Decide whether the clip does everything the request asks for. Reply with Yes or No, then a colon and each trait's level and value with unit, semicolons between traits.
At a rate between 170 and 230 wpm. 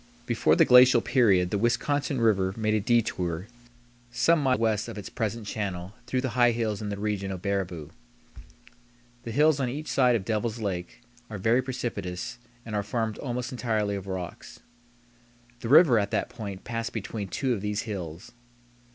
Yes: average, 175 wpm